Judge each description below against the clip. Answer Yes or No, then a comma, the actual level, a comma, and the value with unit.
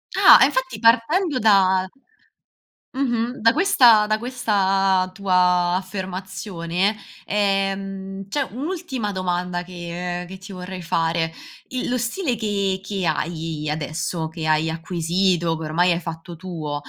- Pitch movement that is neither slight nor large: Yes, average, 3.8 semitones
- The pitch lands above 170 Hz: Yes, high, 190 Hz